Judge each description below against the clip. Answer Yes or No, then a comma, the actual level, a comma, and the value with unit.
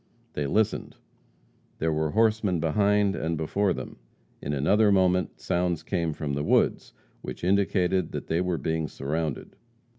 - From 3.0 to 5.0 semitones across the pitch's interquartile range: Yes, average, 4.1 semitones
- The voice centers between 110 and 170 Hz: No, very low, 90 Hz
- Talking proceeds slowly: No, average, 145 wpm